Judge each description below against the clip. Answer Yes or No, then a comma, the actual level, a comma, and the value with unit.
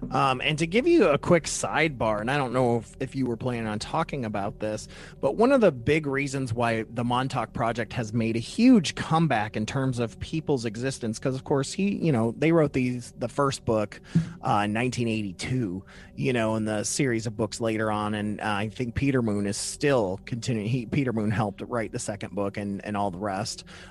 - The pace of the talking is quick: Yes, fast, 220 wpm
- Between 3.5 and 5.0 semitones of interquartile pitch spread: Yes, average, 4.2 semitones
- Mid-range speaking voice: No, low, 120 Hz